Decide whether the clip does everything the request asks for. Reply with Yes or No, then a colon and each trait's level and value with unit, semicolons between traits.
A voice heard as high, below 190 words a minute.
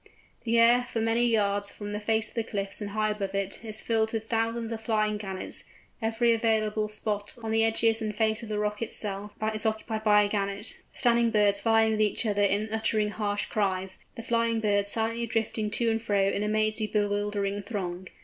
No: high, 215 Hz; fast, 205 wpm